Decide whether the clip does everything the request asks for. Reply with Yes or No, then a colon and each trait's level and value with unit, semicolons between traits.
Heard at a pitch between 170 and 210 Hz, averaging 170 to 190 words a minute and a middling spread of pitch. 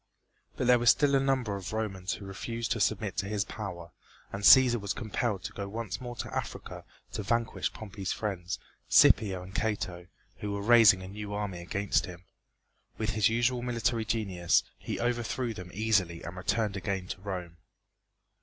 No: low, 105 Hz; average, 175 wpm; average, 3.4 semitones